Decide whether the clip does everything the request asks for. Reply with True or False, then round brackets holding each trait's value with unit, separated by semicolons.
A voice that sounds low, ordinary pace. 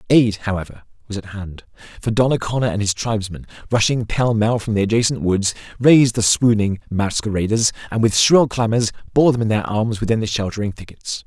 True (110 Hz; 180 wpm)